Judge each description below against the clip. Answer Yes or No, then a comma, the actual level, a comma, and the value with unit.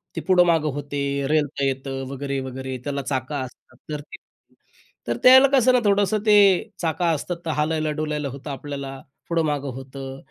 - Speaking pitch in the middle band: Yes, medium, 145 Hz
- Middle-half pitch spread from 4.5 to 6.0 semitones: No, average, 3.4 semitones